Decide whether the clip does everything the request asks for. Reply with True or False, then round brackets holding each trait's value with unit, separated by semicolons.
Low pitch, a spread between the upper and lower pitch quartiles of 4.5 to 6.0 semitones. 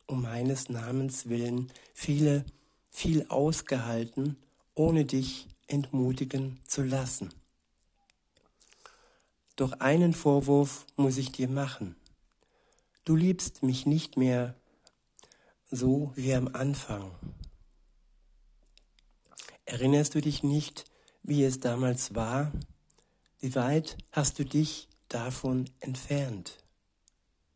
False (130 Hz; 2.9 semitones)